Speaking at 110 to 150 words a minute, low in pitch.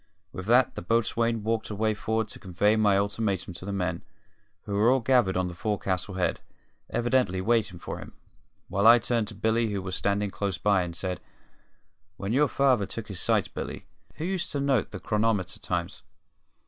No: average, 185 wpm; low, 105 Hz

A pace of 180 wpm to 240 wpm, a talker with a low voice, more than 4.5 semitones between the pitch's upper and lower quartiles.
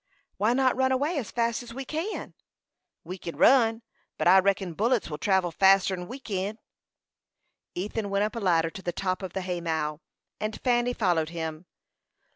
No: average, 185 wpm; high, 195 Hz; average, 5.1 semitones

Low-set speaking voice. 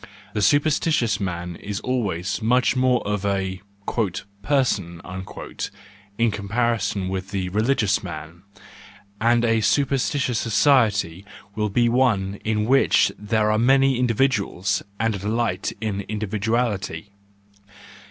Yes: low, 105 Hz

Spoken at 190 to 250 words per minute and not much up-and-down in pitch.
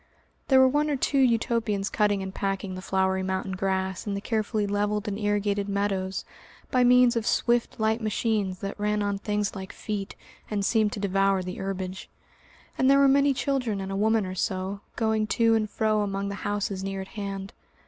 Yes: average, 195 wpm; narrow, 2.2 semitones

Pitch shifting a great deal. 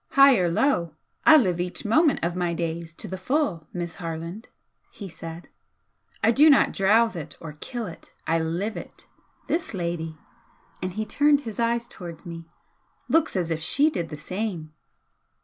Yes: wide, 5.8 semitones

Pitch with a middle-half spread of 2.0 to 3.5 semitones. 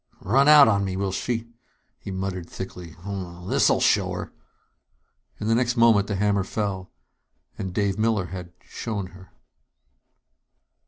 Yes: average, 2.9 semitones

